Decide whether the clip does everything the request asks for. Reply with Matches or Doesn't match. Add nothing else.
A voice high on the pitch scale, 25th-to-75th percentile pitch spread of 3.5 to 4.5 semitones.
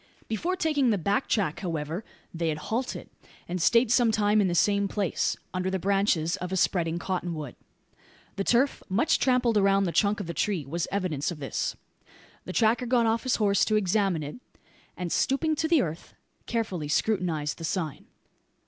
Doesn't match